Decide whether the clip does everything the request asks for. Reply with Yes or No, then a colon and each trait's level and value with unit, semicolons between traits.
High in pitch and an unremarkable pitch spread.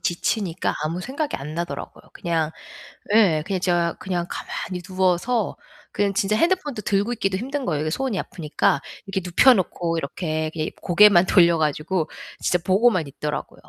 No: medium, 180 Hz; average, 4.1 semitones